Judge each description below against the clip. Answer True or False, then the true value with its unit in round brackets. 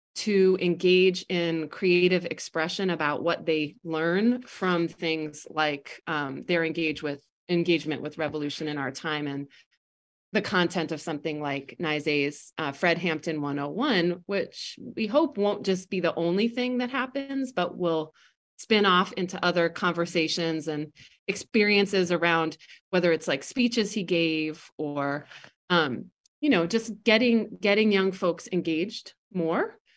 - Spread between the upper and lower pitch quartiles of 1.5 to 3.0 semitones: False (4.2 semitones)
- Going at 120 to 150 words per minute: True (140 wpm)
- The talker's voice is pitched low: False (175 Hz)